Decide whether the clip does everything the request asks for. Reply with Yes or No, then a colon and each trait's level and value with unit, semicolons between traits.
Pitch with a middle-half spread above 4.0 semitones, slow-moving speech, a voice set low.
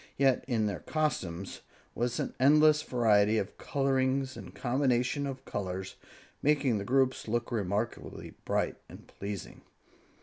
Yes: average, 4.8 semitones; slow, 130 wpm; low, 125 Hz